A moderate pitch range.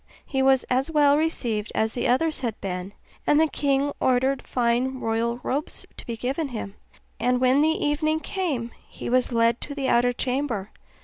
Yes: average, 3.6 semitones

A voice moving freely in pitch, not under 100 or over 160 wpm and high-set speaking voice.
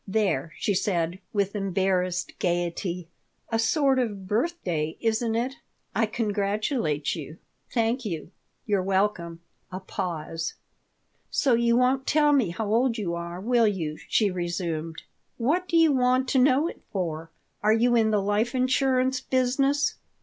Yes: wide, 6.0 semitones; average, 145 wpm; high, 210 Hz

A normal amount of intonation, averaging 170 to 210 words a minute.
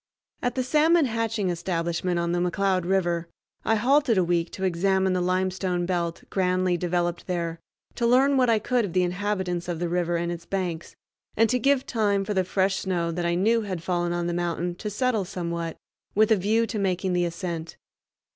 Yes: average, 3.2 semitones; average, 200 wpm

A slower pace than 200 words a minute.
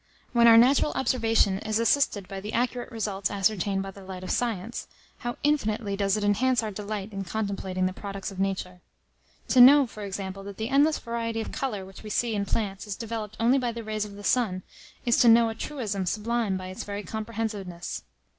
No: fast, 205 wpm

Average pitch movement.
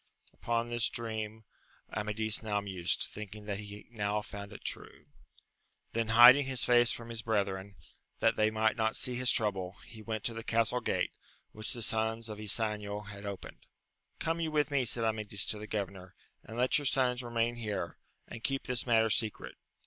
No: narrow, 2.3 semitones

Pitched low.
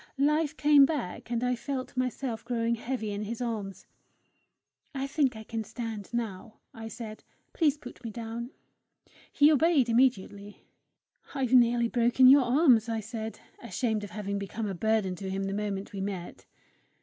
No: high, 230 Hz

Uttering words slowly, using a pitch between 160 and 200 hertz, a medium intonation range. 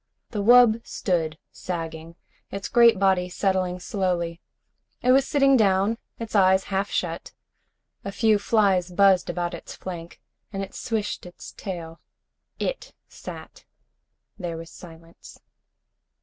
Yes: slow, 125 wpm; high, 190 Hz; average, 3.6 semitones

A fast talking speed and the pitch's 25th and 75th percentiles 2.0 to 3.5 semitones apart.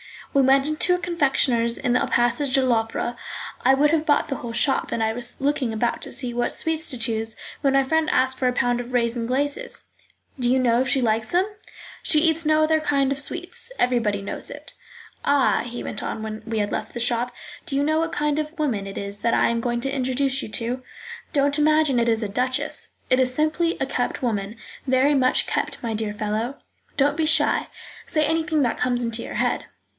No: fast, 220 wpm; average, 4.0 semitones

